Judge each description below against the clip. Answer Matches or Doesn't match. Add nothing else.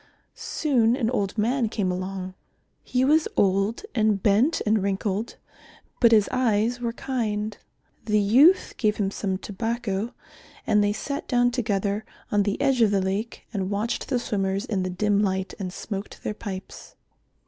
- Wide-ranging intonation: Doesn't match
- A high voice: Matches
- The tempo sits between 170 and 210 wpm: Doesn't match